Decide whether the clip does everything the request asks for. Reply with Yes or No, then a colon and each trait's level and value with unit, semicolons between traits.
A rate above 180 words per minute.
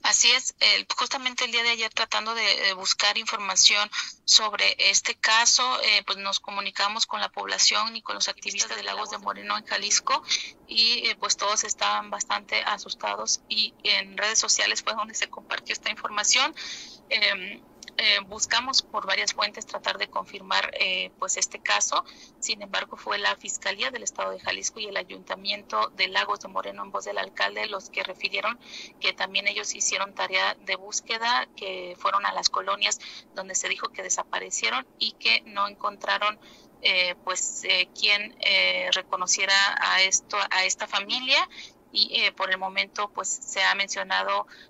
No: average, 165 wpm